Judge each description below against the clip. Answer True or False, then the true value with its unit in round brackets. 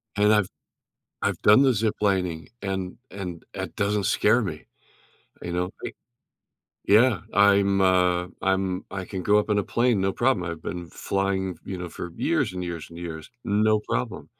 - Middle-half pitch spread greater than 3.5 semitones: False (2.4 semitones)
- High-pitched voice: False (95 Hz)